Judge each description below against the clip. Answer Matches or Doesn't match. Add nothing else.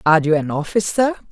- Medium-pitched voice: Matches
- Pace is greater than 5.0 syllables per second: Matches